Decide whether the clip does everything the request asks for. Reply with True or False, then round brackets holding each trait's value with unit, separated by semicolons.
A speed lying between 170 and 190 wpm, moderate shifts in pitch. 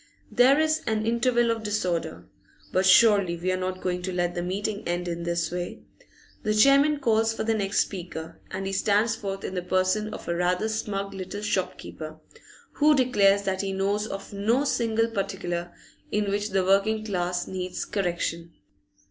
True (175 wpm; 3.3 semitones)